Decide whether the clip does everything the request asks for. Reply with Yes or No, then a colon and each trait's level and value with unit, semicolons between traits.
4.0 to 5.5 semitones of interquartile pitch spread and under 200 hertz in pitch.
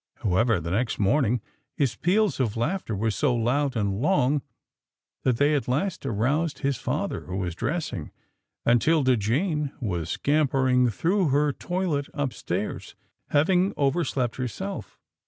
Yes: average, 5.1 semitones; low, 135 Hz